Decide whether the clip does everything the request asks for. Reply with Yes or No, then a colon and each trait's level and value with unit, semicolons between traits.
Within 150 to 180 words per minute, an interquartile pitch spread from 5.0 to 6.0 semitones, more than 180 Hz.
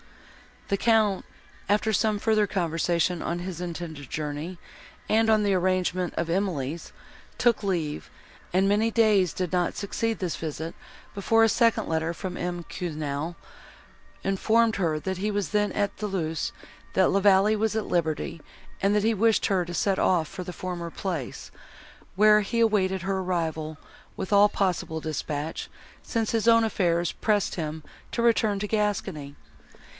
No: average, 155 wpm; average, 3.9 semitones; high, 190 Hz